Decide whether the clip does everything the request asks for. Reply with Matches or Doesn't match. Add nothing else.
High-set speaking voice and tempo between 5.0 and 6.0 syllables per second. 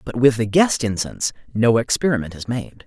Doesn't match